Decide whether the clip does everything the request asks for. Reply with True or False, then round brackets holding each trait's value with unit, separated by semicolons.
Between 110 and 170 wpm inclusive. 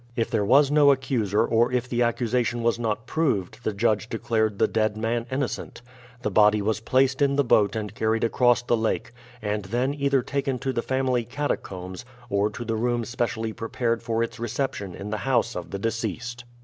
False (195 wpm)